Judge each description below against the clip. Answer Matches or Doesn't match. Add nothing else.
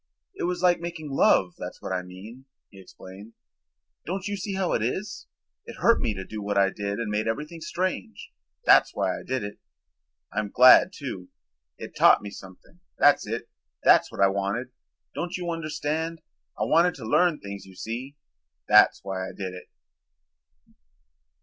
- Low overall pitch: Matches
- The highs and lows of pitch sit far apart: Matches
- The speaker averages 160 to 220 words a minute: Matches